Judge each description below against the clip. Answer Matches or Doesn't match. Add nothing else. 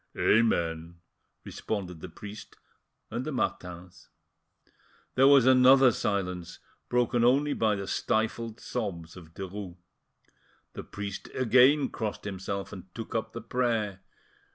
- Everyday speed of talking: Doesn't match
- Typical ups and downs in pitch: Matches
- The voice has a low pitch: Matches